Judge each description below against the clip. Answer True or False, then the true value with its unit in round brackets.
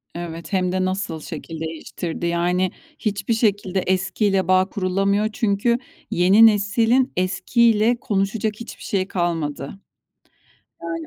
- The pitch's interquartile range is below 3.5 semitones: True (3.1 semitones)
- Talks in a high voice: True (195 Hz)